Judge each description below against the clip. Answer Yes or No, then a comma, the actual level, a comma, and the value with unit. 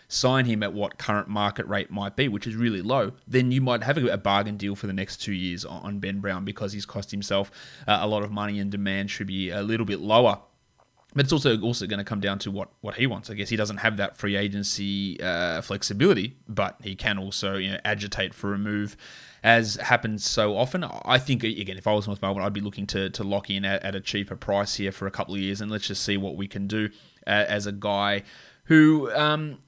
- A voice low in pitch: Yes, low, 100 Hz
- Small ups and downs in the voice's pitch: Yes, narrow, 1.6 semitones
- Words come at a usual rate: No, fast, 245 wpm